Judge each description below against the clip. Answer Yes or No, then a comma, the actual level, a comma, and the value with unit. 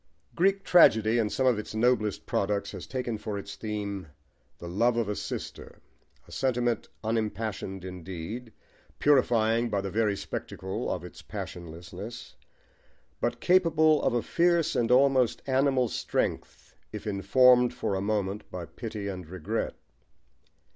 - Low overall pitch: Yes, low, 110 Hz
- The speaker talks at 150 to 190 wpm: No, average, 140 wpm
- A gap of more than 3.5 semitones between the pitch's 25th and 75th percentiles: Yes, average, 4.0 semitones